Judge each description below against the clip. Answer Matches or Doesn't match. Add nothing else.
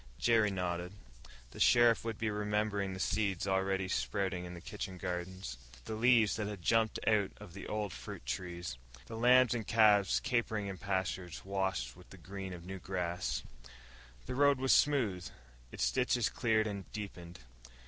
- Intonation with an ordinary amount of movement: Matches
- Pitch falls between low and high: Doesn't match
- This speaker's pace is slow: Doesn't match